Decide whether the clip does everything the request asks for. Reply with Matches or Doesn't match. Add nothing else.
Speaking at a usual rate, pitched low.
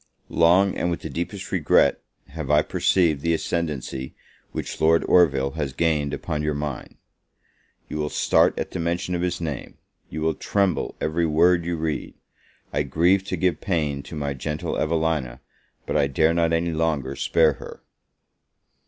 Matches